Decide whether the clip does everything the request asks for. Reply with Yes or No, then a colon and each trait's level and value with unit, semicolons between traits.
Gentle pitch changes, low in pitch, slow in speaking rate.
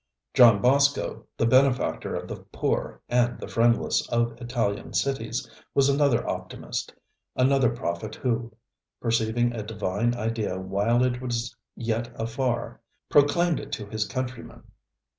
Yes: narrow, 2.3 semitones; low, 120 Hz; slow, 130 wpm